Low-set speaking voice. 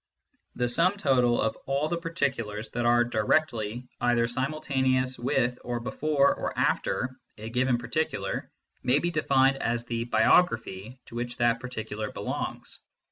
Yes: low, 125 Hz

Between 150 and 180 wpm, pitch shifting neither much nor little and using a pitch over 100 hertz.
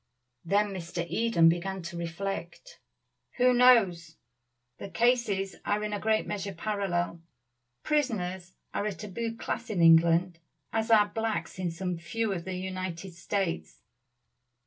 No: slow, 135 wpm; average, 3.9 semitones; high, 190 Hz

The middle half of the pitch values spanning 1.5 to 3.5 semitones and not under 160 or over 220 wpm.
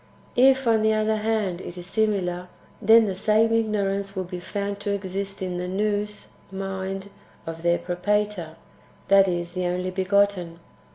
Yes: narrow, 2.5 semitones; average, 165 wpm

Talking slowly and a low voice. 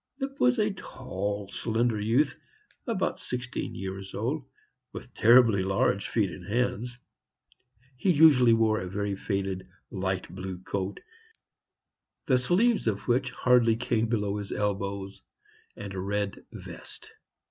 Yes: slow, 130 wpm; low, 110 Hz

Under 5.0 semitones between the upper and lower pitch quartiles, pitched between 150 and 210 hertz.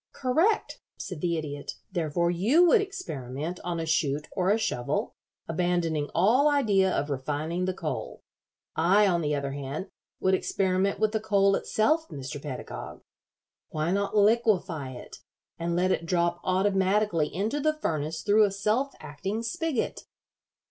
No: wide, 5.4 semitones; medium, 185 Hz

